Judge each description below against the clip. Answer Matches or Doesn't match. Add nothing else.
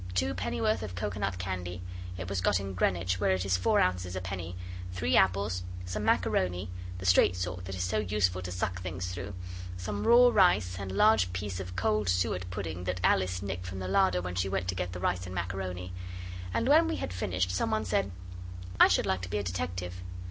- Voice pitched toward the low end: Matches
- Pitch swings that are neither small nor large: Doesn't match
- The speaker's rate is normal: Doesn't match